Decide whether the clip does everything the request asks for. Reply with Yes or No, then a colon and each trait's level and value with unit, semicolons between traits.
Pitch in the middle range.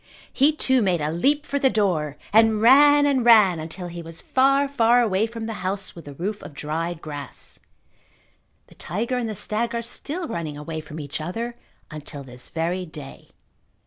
No: high, 195 Hz